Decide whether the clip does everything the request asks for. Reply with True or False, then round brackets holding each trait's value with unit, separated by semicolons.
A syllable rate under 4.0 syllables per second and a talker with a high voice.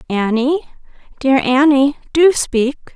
True (3.6 syllables/s; 270 Hz)